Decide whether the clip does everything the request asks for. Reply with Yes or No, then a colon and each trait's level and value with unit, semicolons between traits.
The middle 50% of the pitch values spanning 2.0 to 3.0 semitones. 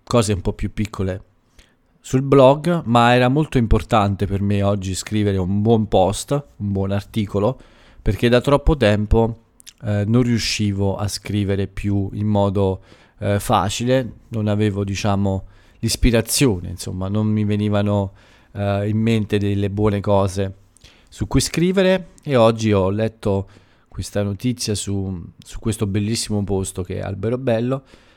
Yes: narrow, 2.5 semitones